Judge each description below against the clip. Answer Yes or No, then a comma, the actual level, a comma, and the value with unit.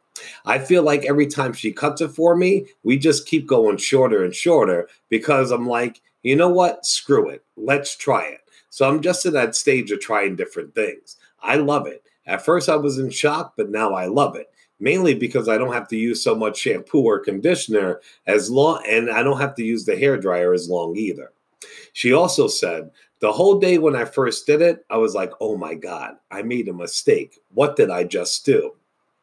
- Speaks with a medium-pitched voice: Yes, medium, 160 Hz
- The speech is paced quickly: Yes, fast, 210 wpm